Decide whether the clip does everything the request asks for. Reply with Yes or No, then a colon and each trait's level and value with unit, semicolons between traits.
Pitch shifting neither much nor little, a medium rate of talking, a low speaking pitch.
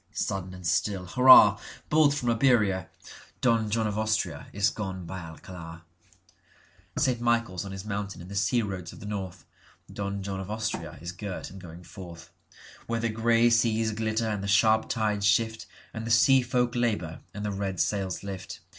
Yes: average, 3.3 semitones; average, 155 wpm; low, 105 Hz